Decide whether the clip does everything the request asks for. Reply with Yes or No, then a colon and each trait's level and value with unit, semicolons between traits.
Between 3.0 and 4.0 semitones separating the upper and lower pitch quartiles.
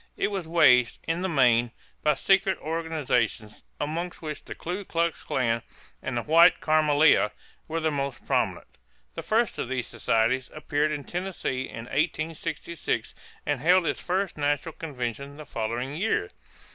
No: average, 4.6 semitones